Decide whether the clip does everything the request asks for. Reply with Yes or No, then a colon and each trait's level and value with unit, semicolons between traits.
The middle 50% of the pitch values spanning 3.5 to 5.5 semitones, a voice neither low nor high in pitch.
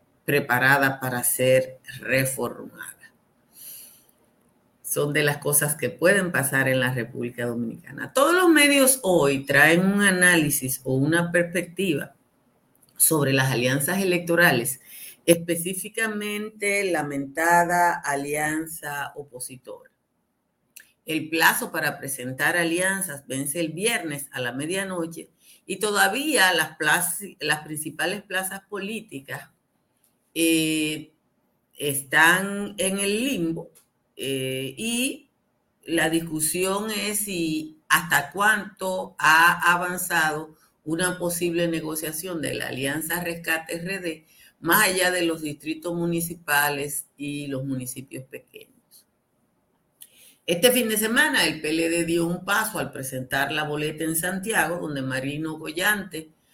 Yes: average, 4.2 semitones; medium, 165 Hz